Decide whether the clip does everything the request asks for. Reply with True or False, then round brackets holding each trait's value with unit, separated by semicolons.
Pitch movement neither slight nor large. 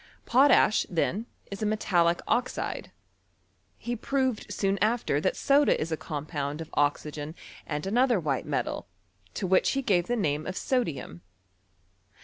False (7.6 semitones)